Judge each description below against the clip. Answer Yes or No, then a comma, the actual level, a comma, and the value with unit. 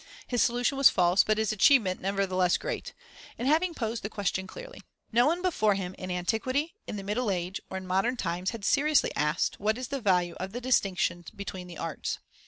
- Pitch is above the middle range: Yes, high, 205 Hz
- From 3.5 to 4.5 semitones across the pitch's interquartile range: No, average, 5.2 semitones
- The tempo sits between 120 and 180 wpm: No, average, 200 wpm